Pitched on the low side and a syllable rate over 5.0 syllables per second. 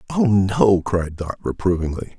No: low, 100 Hz; 4.5 syllables/s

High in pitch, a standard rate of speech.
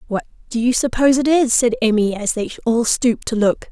No: high, 235 Hz; fast, 225 wpm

